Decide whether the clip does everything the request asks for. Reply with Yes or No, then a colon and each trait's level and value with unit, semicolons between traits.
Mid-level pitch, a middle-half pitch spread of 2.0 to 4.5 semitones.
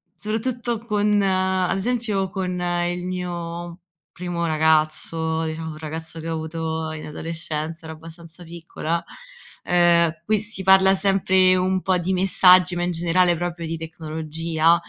Yes: medium, 175 Hz; narrow, 2.6 semitones